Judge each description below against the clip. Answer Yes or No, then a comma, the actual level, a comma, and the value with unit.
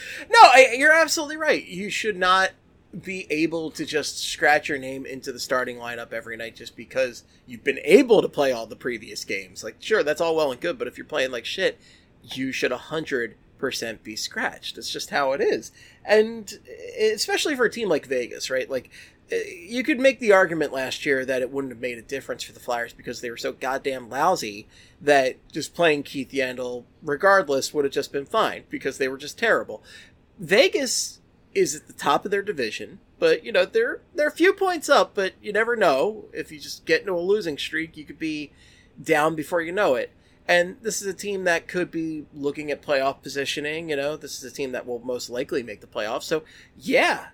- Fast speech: Yes, fast, 210 wpm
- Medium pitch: Yes, medium, 160 Hz